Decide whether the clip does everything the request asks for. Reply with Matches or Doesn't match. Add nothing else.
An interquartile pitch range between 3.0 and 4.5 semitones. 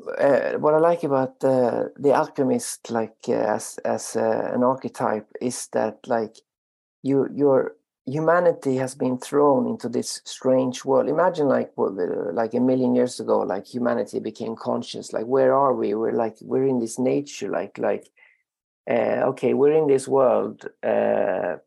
Matches